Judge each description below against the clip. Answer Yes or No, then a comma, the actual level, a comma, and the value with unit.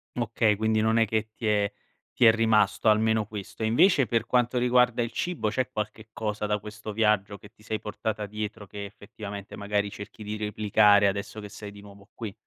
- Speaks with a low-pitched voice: Yes, low, 105 Hz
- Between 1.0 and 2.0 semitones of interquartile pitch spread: Yes, narrow, 1.5 semitones